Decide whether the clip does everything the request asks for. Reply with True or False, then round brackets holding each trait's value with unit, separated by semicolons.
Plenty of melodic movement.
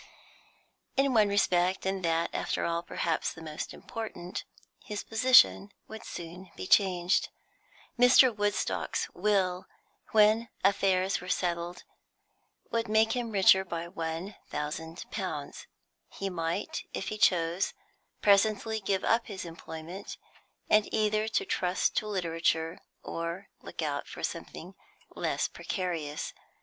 False (3.9 semitones)